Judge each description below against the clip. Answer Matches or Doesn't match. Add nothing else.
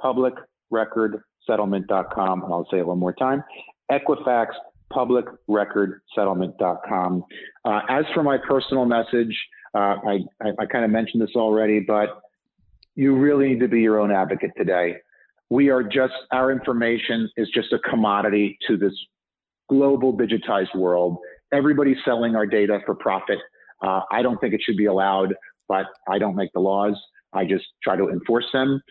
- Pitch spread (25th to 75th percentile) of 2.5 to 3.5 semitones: Doesn't match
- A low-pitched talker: Matches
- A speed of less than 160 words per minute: Doesn't match